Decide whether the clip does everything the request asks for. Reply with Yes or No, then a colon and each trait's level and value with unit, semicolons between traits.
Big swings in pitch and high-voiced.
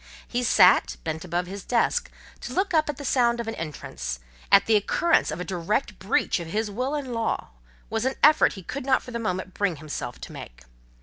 Yes: wide, 6.1 semitones; high, 210 Hz